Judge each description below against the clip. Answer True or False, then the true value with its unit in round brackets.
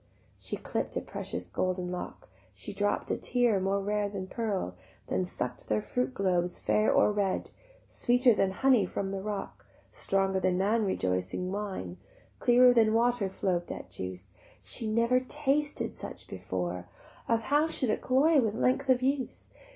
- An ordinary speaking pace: True (160 wpm)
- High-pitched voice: True (200 Hz)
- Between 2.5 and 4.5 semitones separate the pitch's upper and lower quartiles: False (5.1 semitones)